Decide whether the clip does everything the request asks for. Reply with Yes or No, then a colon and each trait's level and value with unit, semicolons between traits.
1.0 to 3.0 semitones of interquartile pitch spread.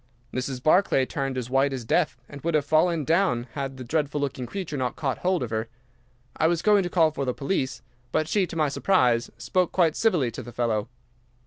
No: average, 4.9 semitones